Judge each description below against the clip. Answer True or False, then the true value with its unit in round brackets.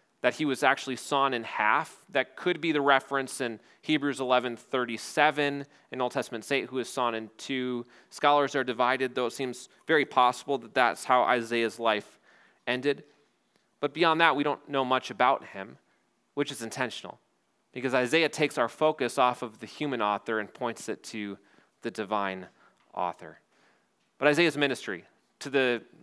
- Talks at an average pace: True (170 wpm)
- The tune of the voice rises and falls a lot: False (3.1 semitones)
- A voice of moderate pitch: False (130 Hz)